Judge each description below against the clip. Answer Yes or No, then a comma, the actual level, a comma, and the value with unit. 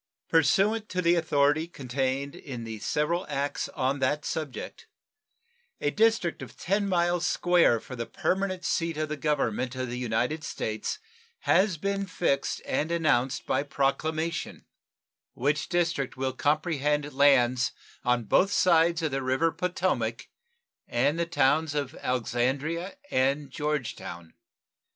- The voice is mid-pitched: Yes, medium, 150 Hz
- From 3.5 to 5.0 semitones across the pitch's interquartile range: Yes, average, 4.5 semitones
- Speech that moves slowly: Yes, slow, 130 wpm